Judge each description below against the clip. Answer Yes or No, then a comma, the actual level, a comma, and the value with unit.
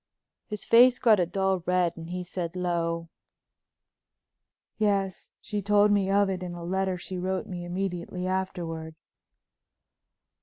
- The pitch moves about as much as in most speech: No, narrow, 2.0 semitones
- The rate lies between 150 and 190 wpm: No, average, 140 wpm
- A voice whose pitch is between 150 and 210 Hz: Yes, medium, 185 Hz